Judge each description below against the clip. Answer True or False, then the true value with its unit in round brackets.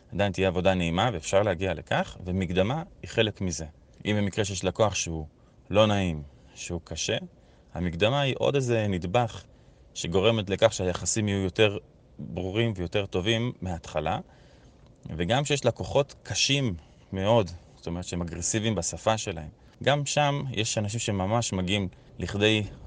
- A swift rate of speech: False (135 wpm)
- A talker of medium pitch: False (100 Hz)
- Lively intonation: False (4.2 semitones)